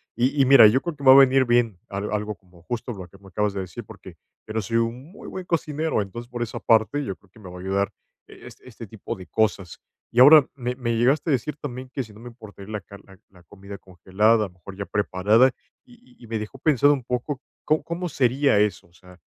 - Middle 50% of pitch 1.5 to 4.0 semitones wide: No, average, 5.0 semitones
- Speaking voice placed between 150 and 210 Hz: No, low, 115 Hz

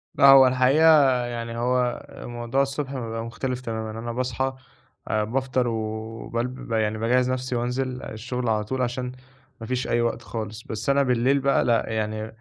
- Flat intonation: Yes, narrow, 2.2 semitones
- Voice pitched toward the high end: No, low, 120 Hz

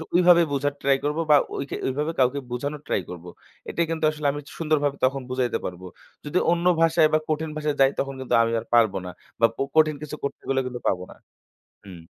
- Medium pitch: Yes, medium, 145 Hz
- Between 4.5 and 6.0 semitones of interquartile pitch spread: No, average, 3.2 semitones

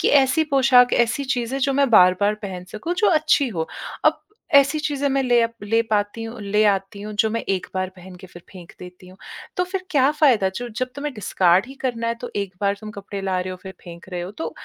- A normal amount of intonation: No, wide, 5.8 semitones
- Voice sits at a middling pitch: No, high, 220 Hz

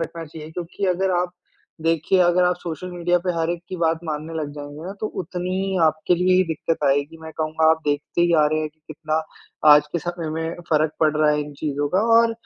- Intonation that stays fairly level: Yes, narrow, 2.3 semitones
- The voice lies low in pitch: No, medium, 160 Hz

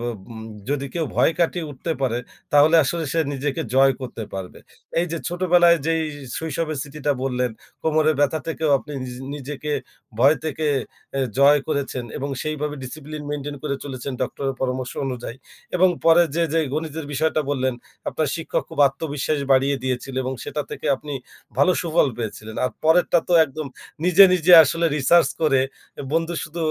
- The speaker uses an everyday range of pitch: Yes, average, 3.2 semitones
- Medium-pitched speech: Yes, medium, 150 Hz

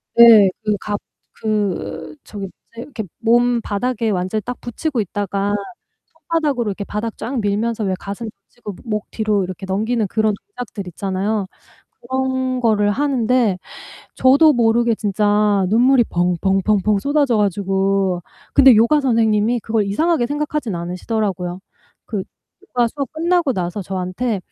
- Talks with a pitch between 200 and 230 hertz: Yes, high, 215 Hz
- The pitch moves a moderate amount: Yes, average, 3.7 semitones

